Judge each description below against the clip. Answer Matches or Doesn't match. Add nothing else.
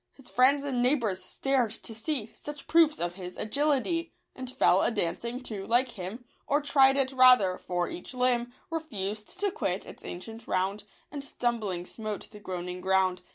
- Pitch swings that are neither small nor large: Doesn't match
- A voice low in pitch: Doesn't match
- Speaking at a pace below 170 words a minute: Doesn't match